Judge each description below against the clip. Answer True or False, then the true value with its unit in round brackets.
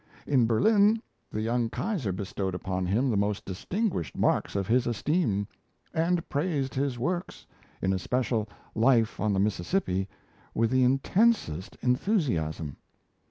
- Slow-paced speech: True (130 wpm)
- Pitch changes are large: True (7.5 semitones)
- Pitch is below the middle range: True (120 Hz)